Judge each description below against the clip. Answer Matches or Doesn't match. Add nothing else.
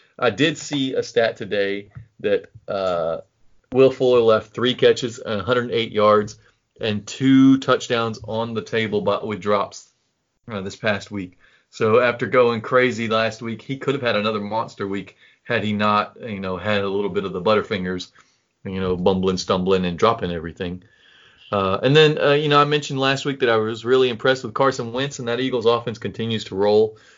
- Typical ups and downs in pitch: Matches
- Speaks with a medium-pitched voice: Doesn't match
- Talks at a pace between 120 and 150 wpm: Doesn't match